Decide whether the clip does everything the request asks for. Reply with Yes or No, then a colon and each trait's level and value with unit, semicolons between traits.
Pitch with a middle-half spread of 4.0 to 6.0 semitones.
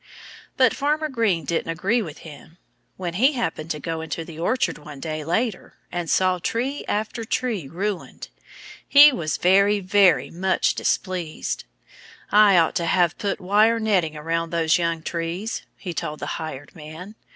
Yes: average, 4.6 semitones